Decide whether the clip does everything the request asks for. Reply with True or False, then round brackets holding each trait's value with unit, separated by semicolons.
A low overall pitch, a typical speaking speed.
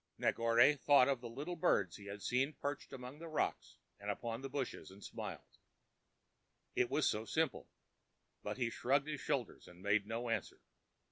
True (125 Hz; 175 wpm)